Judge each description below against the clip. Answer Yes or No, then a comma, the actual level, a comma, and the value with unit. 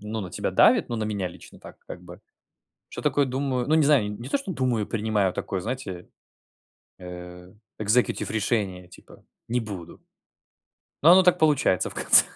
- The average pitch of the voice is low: Yes, low, 110 Hz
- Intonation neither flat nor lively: No, wide, 5.9 semitones